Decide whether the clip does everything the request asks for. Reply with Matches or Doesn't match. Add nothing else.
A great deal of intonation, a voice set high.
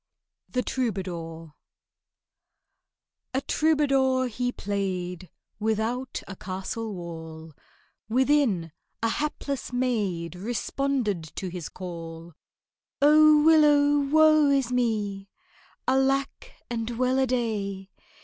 Matches